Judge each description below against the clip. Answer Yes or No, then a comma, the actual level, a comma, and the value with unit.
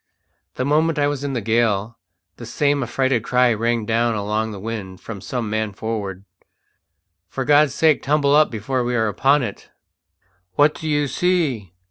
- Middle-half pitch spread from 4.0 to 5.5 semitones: Yes, average, 4.7 semitones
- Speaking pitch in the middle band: No, low, 120 Hz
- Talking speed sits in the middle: Yes, average, 170 wpm